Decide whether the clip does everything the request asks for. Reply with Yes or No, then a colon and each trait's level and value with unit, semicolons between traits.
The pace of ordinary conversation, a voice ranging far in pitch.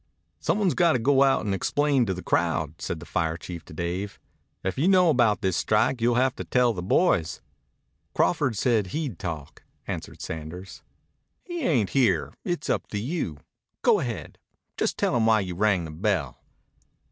Yes: average, 180 wpm; wide, 7.1 semitones